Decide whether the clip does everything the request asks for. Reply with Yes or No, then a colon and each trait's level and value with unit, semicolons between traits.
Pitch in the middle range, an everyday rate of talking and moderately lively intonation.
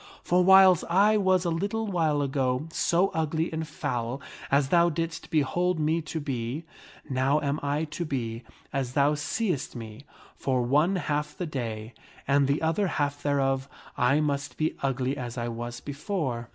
Yes: medium, 145 Hz; average, 165 wpm; average, 3.9 semitones